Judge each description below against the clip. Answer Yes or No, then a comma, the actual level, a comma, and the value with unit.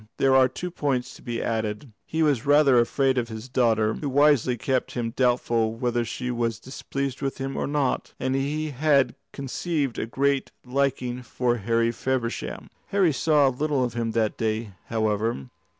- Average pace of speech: Yes, average, 170 wpm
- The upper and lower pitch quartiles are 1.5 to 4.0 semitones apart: Yes, average, 3.1 semitones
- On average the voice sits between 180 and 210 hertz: No, low, 125 Hz